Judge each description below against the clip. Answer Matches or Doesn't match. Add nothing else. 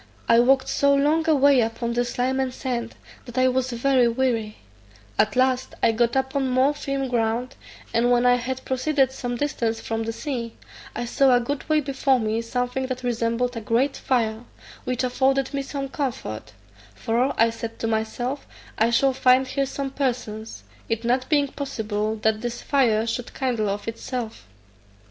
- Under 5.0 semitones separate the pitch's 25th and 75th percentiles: Matches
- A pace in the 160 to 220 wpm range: Matches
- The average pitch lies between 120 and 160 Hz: Doesn't match